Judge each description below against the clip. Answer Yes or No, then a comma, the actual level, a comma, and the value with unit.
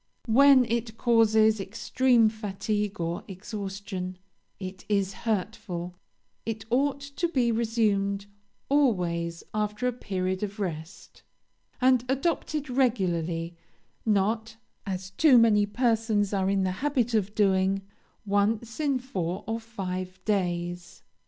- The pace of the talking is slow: Yes, slow, 115 wpm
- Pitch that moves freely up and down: No, average, 3.7 semitones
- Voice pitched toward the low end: No, high, 210 Hz